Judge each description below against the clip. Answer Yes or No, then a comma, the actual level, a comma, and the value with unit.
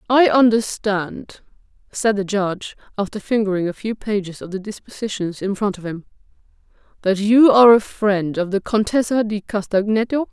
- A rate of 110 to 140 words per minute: No, average, 155 wpm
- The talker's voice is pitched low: No, high, 205 Hz